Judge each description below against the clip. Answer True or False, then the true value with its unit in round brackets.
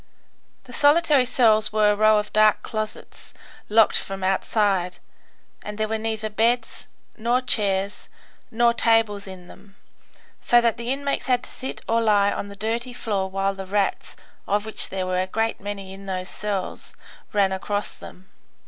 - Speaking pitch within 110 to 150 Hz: False (210 Hz)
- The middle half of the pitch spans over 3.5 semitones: False (2.7 semitones)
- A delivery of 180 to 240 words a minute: False (165 wpm)